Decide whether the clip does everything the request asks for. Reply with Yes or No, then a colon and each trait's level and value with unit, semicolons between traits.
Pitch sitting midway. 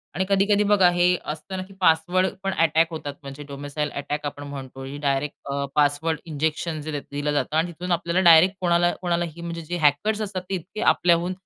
Yes: medium, 165 Hz